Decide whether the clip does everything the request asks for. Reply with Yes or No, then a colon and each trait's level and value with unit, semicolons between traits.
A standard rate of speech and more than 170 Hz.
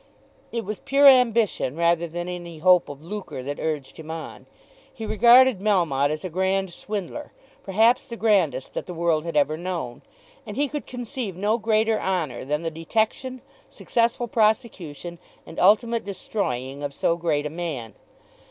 Yes: average, 160 wpm; medium, 185 Hz